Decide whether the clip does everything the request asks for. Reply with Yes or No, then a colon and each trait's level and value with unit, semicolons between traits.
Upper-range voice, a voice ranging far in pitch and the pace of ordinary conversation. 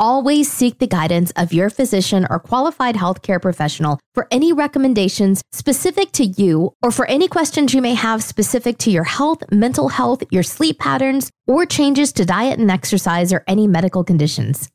Yes: high, 220 Hz; wide, 6.7 semitones; average, 175 wpm